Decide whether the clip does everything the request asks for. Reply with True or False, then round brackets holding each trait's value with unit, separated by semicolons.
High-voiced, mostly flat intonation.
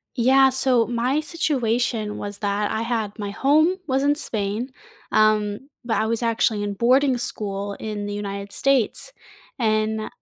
False (225 Hz; 4.1 semitones)